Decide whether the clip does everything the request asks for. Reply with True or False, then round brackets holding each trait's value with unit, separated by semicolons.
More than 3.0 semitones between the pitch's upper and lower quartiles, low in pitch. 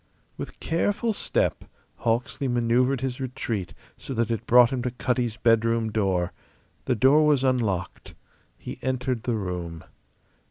False (2.7 semitones; 120 Hz)